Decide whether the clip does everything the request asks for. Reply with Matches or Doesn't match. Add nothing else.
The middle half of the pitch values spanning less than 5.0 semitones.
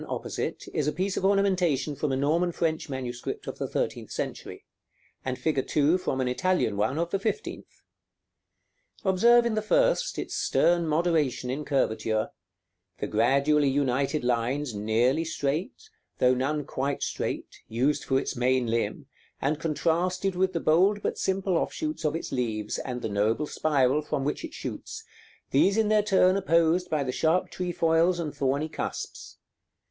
Doesn't match